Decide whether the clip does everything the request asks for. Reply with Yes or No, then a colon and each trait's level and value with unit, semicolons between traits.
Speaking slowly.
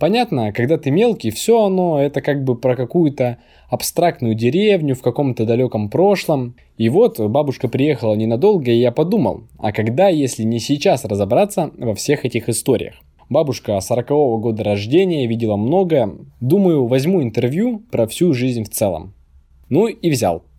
No: average, 150 wpm